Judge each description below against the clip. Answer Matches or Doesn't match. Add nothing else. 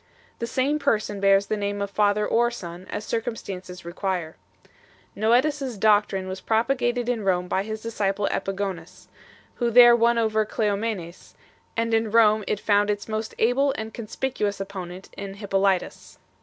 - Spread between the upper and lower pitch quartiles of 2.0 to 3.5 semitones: Matches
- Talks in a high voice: Matches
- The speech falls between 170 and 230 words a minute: Doesn't match